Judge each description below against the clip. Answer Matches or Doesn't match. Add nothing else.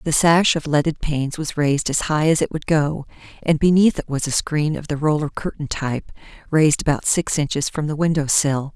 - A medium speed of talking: Doesn't match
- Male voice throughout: Doesn't match